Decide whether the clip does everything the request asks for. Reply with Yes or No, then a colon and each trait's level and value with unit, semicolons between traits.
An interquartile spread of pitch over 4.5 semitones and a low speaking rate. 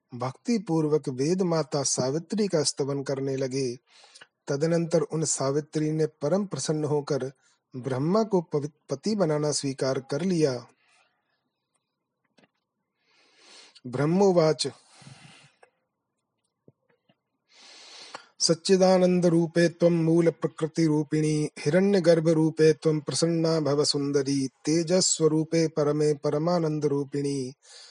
No: average, 2.8 semitones; slow, 85 wpm